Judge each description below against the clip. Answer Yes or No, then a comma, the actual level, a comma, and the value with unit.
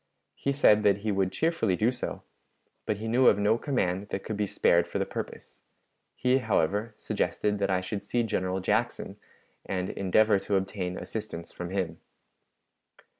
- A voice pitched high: No, low, 100 Hz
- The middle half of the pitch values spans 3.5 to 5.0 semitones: No, average, 2.9 semitones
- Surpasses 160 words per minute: Yes, average, 170 wpm